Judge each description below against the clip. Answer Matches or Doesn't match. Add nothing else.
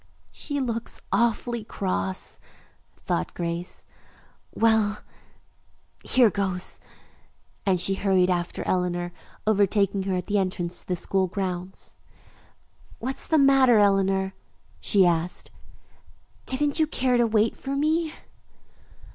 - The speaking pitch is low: Doesn't match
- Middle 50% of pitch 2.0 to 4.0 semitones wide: Doesn't match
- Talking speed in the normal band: Doesn't match